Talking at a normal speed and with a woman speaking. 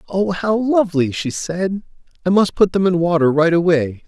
No: average, 190 wpm; male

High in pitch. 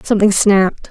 Yes: high, 200 Hz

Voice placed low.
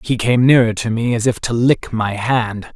Yes: low, 115 Hz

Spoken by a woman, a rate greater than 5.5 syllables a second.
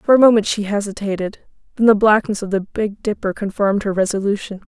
Yes: female; 6.0 syllables/s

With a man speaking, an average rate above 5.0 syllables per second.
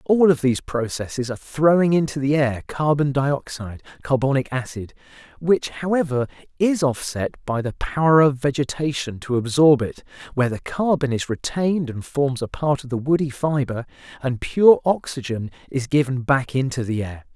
No: male; 4.9 syllables/s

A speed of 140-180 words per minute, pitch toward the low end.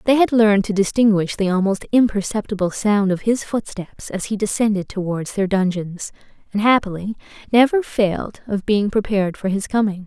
No: average, 165 wpm; high, 205 Hz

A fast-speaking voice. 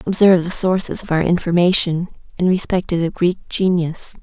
No: average, 170 wpm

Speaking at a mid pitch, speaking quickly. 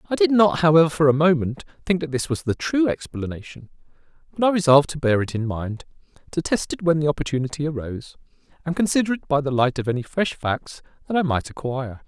Yes: medium, 155 Hz; fast, 215 wpm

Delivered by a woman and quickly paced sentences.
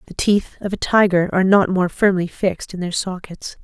Yes: female; fast, 215 wpm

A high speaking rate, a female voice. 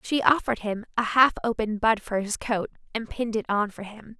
Yes: fast, 230 wpm; female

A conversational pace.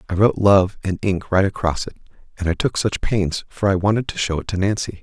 No: fast, 250 wpm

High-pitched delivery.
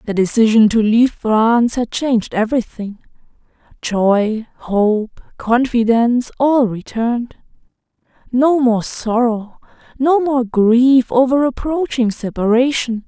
Yes: high, 240 Hz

